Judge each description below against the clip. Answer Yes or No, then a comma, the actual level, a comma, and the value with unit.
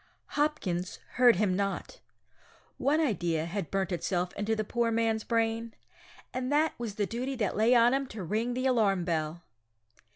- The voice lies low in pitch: No, high, 220 Hz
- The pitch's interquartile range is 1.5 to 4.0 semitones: No, average, 4.4 semitones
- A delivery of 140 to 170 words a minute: Yes, average, 165 wpm